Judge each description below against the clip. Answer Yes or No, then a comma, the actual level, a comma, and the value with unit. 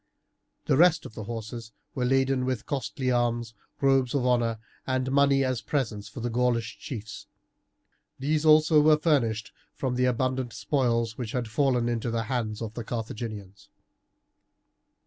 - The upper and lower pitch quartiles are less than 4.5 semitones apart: Yes, average, 2.8 semitones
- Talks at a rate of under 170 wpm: Yes, average, 150 wpm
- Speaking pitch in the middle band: No, low, 125 Hz